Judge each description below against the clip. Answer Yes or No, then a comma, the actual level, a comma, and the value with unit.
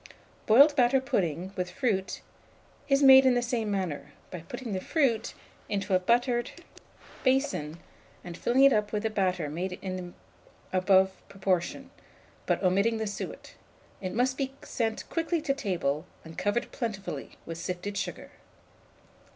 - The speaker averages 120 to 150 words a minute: Yes, average, 145 wpm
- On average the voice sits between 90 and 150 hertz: No, high, 205 Hz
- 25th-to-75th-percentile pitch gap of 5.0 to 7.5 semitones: Yes, wide, 5.4 semitones